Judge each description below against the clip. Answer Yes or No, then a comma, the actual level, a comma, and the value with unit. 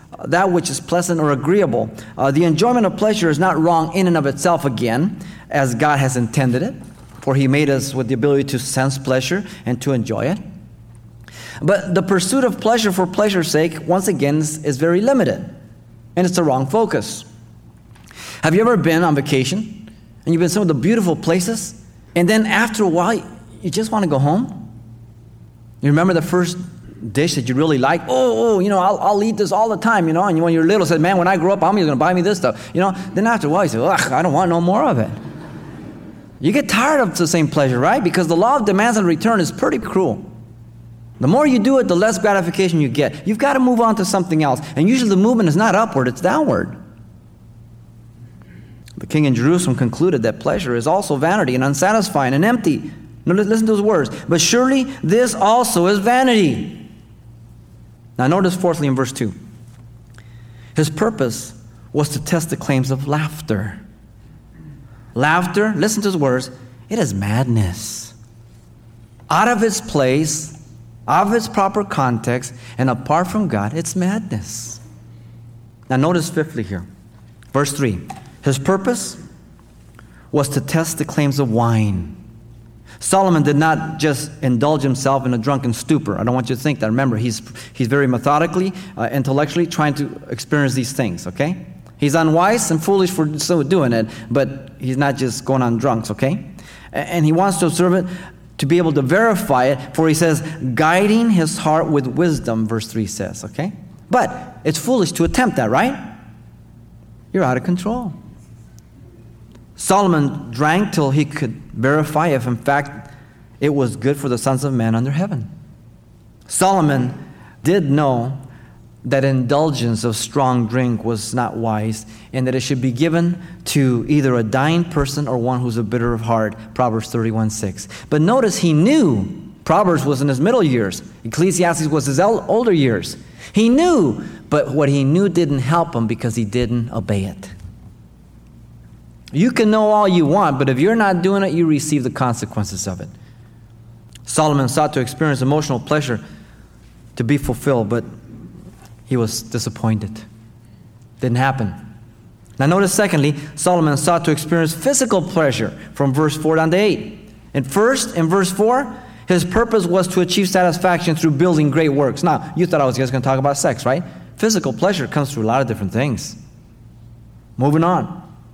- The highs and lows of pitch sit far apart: Yes, wide, 7.1 semitones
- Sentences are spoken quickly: No, average, 180 wpm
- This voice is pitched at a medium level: Yes, medium, 145 Hz